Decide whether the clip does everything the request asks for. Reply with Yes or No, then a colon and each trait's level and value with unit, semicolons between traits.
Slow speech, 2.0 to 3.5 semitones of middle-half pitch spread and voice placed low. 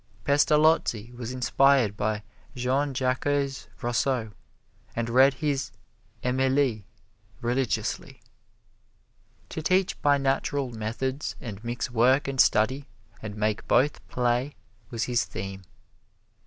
Yes: slow, 105 wpm; average, 2.9 semitones; low, 130 Hz